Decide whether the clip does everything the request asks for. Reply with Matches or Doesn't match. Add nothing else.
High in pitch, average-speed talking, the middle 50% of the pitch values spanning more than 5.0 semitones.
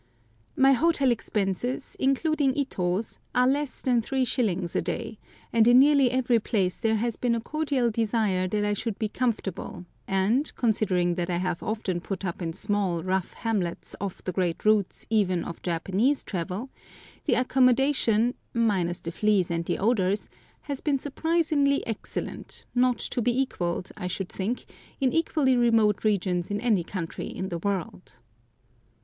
Matches